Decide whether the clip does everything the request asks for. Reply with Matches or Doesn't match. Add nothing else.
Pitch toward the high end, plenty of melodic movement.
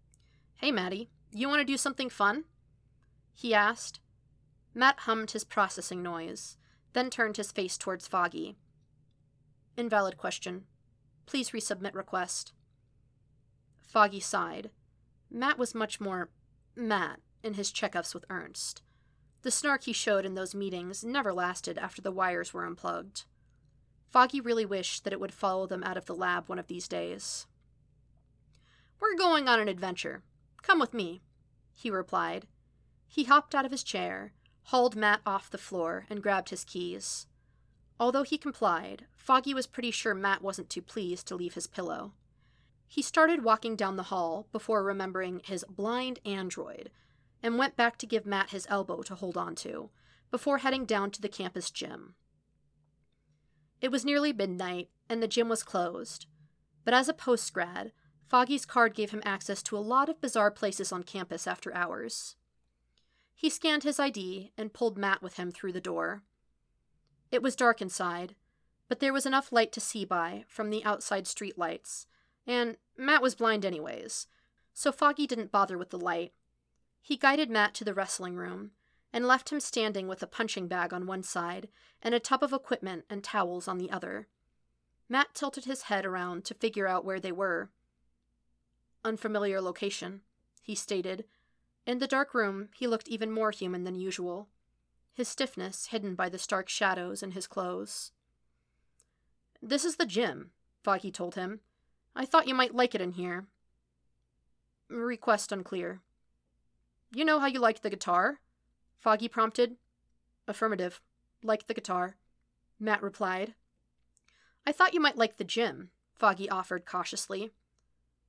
Doesn't match